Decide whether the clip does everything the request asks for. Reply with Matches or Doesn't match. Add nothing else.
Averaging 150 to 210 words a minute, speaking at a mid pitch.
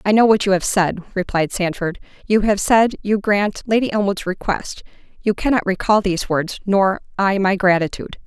Doesn't match